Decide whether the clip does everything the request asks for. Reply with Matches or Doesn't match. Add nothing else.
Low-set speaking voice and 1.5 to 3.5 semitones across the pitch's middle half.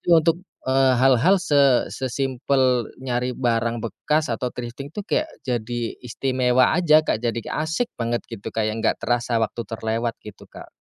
Matches